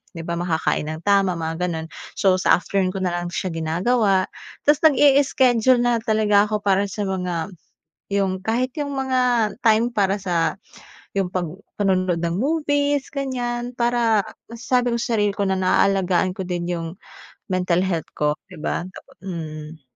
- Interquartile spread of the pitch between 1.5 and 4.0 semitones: No, average, 5.3 semitones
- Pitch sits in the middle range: No, high, 195 Hz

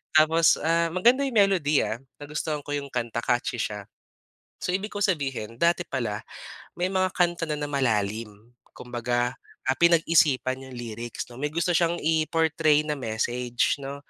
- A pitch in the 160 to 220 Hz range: No, medium, 145 Hz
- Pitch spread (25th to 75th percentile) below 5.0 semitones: No, wide, 5.5 semitones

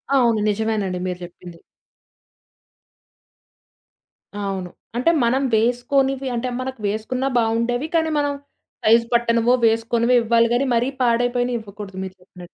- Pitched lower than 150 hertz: No, high, 235 Hz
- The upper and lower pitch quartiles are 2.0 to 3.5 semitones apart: Yes, average, 2.7 semitones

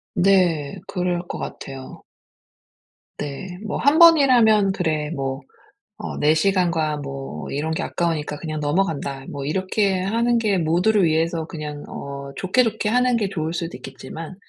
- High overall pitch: No, medium, 170 Hz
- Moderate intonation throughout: Yes, average, 4.8 semitones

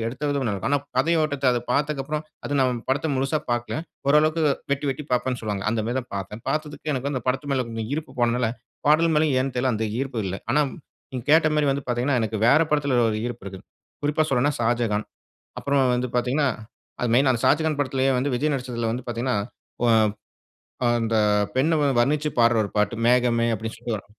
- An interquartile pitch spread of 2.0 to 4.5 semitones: Yes, average, 3.4 semitones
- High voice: No, low, 130 Hz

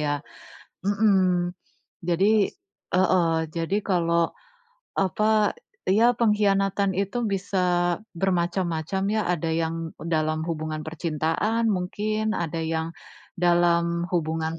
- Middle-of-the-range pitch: Yes, medium, 175 Hz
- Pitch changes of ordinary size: Yes, average, 3.2 semitones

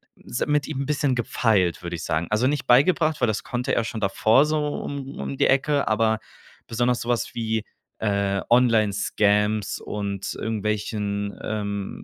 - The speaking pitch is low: Yes, low, 110 Hz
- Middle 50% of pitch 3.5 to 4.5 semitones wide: Yes, average, 4.1 semitones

